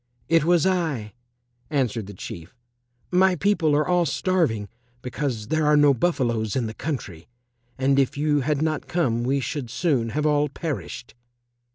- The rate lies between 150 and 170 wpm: Yes, average, 160 wpm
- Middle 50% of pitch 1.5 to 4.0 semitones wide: No, average, 5.0 semitones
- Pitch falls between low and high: Yes, medium, 145 Hz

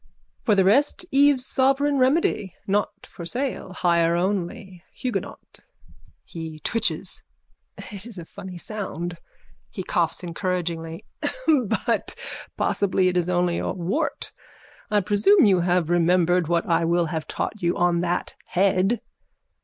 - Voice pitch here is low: No, medium, 185 Hz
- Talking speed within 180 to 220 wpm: No, slow, 135 wpm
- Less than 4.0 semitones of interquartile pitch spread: Yes, average, 3.5 semitones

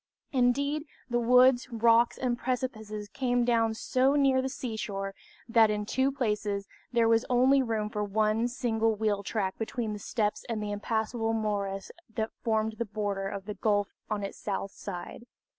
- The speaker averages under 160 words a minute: No, average, 165 wpm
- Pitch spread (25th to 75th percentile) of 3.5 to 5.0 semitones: No, average, 2.8 semitones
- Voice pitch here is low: No, high, 225 Hz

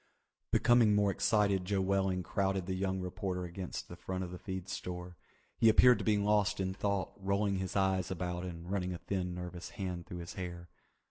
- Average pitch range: No, narrow, 1.9 semitones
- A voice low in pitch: Yes, very low, 95 Hz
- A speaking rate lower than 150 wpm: No, average, 195 wpm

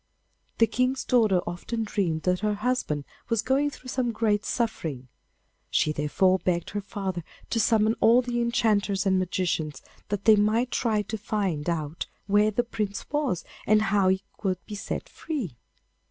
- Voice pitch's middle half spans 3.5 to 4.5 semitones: Yes, average, 3.8 semitones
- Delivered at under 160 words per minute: No, average, 165 wpm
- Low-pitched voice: No, high, 205 Hz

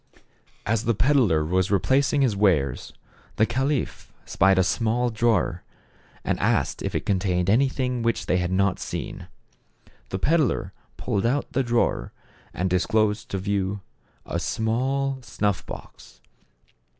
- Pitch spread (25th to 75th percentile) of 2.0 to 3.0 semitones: No, average, 4.9 semitones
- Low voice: Yes, low, 110 Hz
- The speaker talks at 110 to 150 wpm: Yes, average, 140 wpm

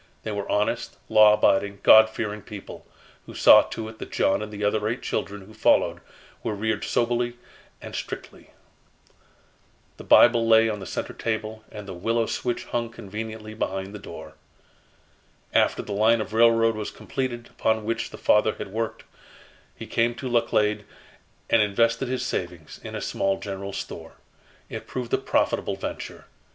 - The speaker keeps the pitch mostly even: Yes, narrow, 2.0 semitones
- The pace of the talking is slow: No, average, 165 wpm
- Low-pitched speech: Yes, low, 110 Hz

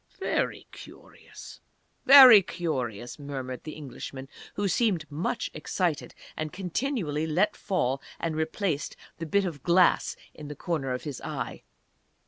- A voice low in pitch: No, medium, 160 Hz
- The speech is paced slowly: Yes, slow, 130 wpm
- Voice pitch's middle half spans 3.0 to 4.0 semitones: No, average, 4.5 semitones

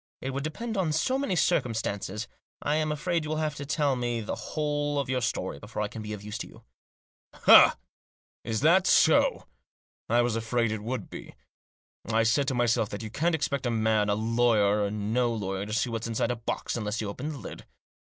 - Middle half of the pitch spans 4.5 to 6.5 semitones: Yes, average, 5.2 semitones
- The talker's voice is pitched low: Yes, low, 120 Hz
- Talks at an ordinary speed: No, fast, 210 wpm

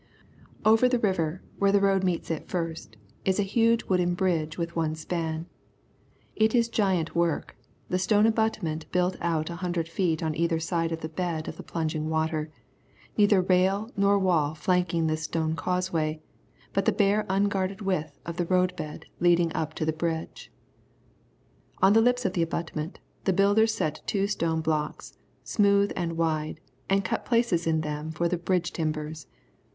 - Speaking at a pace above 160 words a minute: Yes, average, 170 wpm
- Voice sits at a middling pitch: Yes, medium, 170 Hz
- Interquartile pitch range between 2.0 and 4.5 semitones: Yes, average, 3.5 semitones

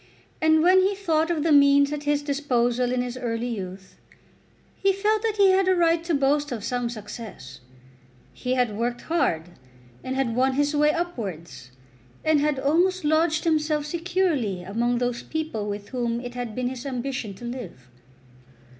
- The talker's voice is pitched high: Yes, very high, 270 Hz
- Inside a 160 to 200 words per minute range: Yes, average, 170 wpm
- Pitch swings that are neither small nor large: Yes, average, 5.0 semitones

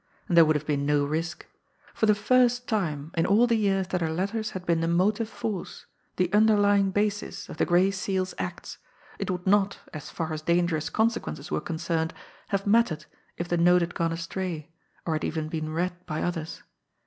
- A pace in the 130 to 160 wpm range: No, average, 195 wpm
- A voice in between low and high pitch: Yes, medium, 180 Hz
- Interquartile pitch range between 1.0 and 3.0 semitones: No, average, 3.9 semitones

